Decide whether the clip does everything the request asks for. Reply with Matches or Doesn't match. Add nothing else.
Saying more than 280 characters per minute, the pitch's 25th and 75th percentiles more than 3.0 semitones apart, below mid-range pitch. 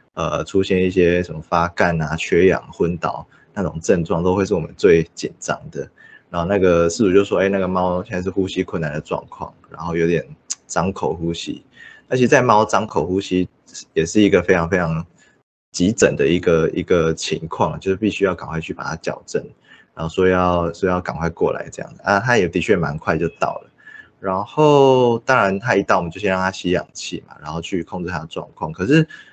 Doesn't match